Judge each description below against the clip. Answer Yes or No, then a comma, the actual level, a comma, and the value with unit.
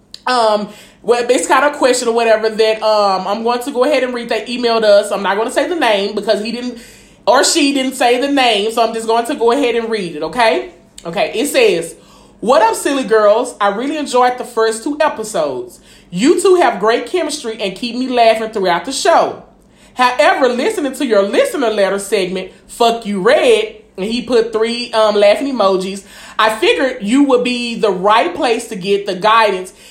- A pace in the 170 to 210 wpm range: Yes, fast, 205 wpm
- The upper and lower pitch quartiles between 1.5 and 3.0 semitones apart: No, average, 3.5 semitones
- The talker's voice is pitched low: No, high, 230 Hz